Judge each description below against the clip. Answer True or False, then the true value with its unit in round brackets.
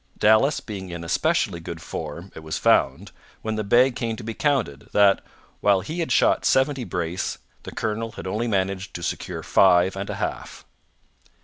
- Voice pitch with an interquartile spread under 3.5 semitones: False (4.5 semitones)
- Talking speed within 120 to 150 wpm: False (180 wpm)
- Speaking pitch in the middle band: False (100 Hz)